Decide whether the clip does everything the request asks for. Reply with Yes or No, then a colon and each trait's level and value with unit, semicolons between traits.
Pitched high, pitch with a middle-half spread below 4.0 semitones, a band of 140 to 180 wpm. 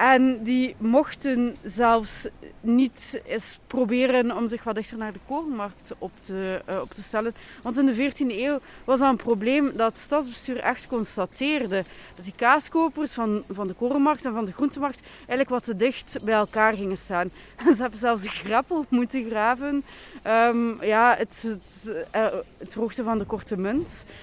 Yes: high, 235 Hz; average, 3.4 semitones; average, 170 wpm